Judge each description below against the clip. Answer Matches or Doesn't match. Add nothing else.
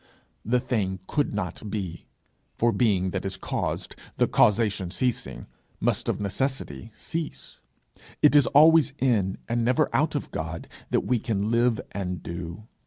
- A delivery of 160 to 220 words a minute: Doesn't match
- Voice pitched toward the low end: Matches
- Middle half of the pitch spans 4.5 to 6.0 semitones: Matches